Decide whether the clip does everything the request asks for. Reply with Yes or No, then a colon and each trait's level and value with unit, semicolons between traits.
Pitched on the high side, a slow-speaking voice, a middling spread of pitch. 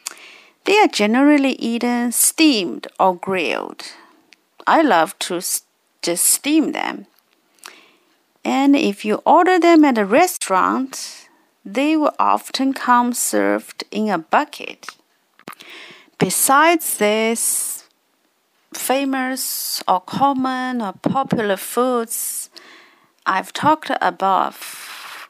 No: very high, 265 Hz; slow, 95 wpm; wide, 6.0 semitones